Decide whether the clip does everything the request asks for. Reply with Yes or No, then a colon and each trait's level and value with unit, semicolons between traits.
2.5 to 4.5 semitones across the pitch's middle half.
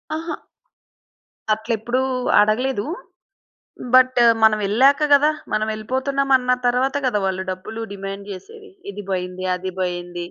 No: average, 5.1 semitones